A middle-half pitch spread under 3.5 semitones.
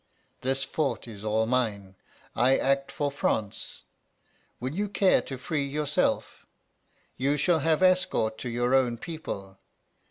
No: average, 4.6 semitones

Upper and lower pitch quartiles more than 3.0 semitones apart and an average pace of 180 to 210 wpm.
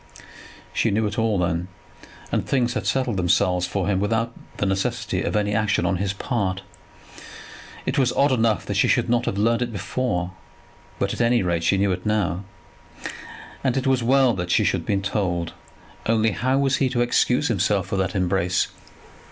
Yes: average, 4.3 semitones; average, 190 wpm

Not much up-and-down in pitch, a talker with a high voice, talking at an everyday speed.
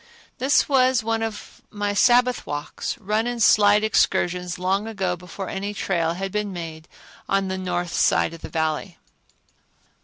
No: average, 3.6 semitones; high, 195 Hz; average, 155 wpm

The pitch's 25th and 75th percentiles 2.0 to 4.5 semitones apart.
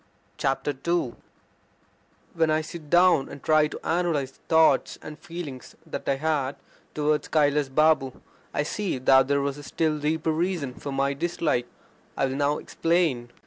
Yes: average, 2.8 semitones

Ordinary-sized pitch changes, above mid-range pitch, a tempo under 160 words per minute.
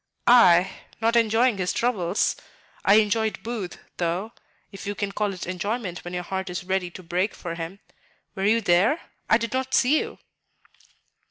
No: average, 4.1 semitones; high, 200 Hz; average, 170 wpm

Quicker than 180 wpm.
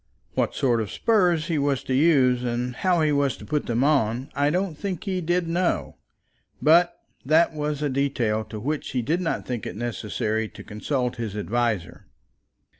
Yes: average, 190 wpm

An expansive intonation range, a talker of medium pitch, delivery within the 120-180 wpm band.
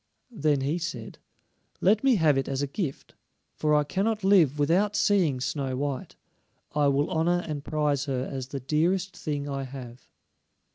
No: average, 4.4 semitones; medium, 150 Hz; average, 170 wpm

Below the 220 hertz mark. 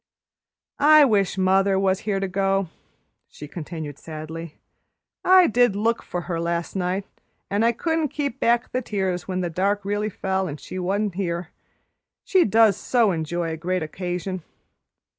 Yes: high, 190 Hz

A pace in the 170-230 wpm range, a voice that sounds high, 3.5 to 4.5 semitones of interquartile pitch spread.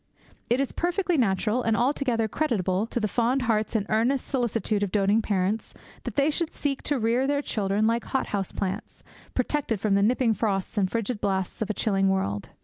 Yes: average, 195 wpm; high, 225 Hz; average, 4.1 semitones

